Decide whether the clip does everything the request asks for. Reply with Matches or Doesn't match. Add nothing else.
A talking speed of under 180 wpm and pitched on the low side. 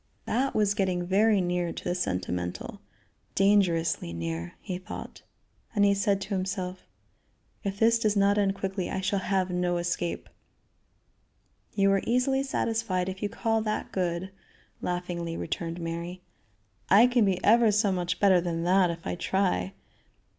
Doesn't match